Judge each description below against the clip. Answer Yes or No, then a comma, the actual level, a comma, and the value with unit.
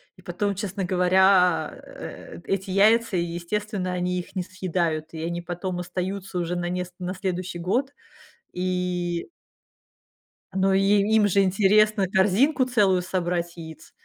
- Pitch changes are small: Yes, narrow, 2.0 semitones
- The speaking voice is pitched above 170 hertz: Yes, medium, 185 Hz